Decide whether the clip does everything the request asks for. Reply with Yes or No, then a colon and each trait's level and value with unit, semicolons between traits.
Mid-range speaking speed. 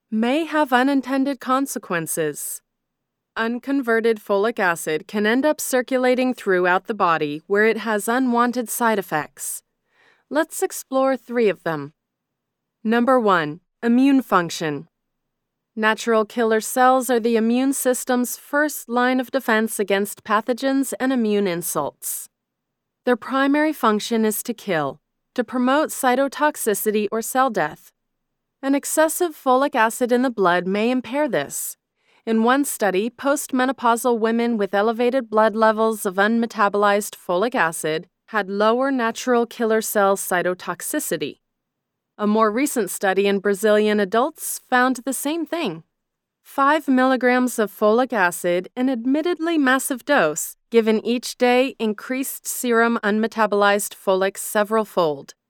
No: slow, 125 wpm